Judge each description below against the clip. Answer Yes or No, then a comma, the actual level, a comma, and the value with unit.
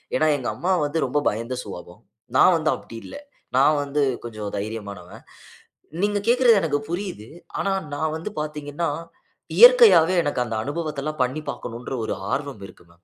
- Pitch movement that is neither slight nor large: No, wide, 6.1 semitones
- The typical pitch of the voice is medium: Yes, medium, 145 Hz